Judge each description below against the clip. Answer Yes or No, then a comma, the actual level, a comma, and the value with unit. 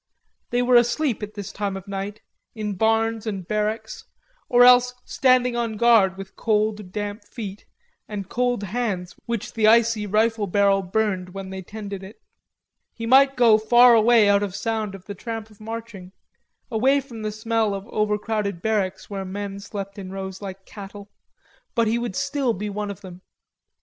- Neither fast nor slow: Yes, average, 175 wpm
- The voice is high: Yes, high, 210 Hz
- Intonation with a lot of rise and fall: No, narrow, 2.6 semitones